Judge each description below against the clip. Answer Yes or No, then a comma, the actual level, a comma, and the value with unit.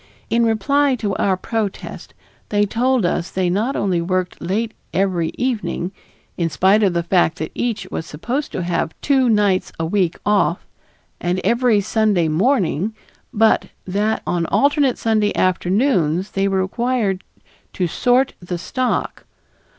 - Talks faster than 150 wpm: No, average, 145 wpm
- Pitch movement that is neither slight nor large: Yes, average, 4.5 semitones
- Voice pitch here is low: No, high, 200 Hz